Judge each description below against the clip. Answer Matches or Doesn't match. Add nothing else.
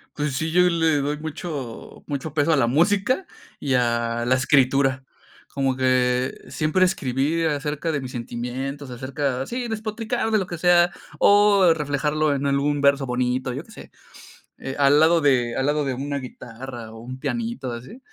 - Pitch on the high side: Doesn't match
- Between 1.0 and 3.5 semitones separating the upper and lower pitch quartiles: Doesn't match